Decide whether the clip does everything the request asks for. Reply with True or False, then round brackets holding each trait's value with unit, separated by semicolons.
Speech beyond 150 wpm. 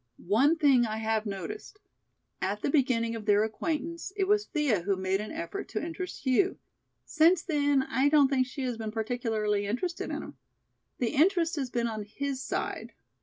True (180 wpm)